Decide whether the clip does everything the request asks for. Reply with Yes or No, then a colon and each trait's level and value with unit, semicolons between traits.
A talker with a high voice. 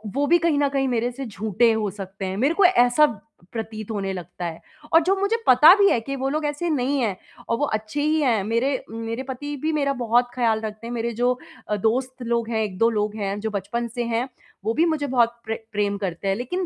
Yes: high, 235 Hz